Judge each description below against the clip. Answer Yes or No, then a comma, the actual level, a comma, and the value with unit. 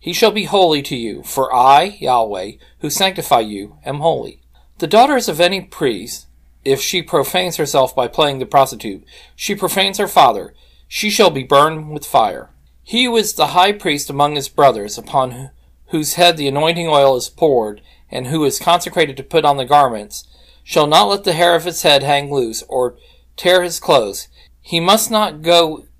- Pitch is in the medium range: Yes, medium, 150 Hz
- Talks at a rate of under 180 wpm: No, average, 190 wpm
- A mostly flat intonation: No, average, 5.1 semitones